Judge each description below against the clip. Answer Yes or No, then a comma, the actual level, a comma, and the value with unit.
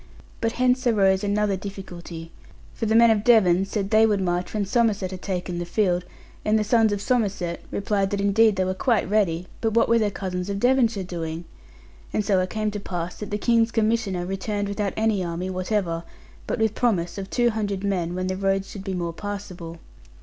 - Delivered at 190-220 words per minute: Yes, fast, 205 wpm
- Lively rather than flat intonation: No, average, 2.9 semitones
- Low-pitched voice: No, high, 200 Hz